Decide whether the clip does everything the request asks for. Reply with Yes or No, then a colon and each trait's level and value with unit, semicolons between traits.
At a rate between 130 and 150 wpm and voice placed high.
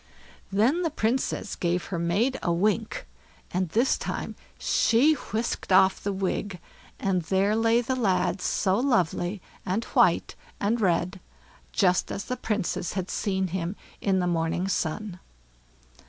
Yes: average, 140 wpm; high, 195 Hz